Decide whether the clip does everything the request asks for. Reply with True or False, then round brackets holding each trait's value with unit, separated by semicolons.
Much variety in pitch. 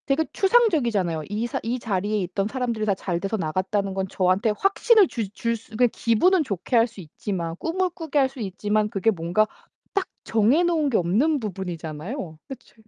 True (6.2 semitones)